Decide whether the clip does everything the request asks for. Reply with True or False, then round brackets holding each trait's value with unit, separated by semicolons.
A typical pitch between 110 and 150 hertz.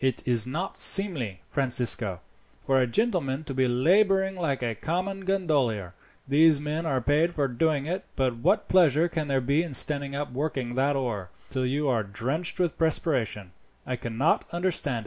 True (140 Hz)